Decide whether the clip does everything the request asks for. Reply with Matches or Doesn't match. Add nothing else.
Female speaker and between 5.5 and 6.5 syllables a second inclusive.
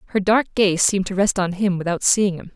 Matches